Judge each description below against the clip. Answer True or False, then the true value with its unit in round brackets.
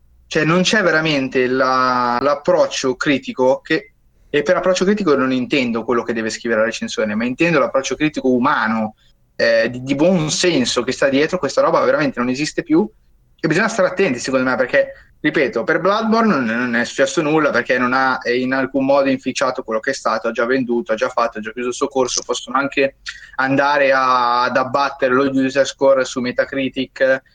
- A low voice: True (130 Hz)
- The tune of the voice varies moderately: True (3.7 semitones)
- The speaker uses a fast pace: True (190 wpm)